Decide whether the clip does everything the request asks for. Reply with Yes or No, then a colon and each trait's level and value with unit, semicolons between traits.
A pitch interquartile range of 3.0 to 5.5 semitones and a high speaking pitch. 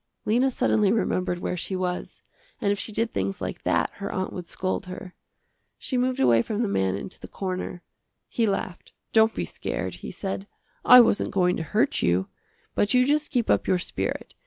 Yes: average, 4.0 semitones; high, 195 Hz